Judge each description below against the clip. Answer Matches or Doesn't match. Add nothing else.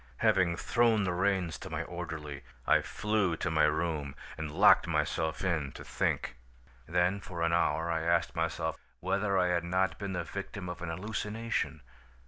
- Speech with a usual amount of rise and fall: Matches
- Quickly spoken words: Doesn't match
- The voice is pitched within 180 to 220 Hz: Doesn't match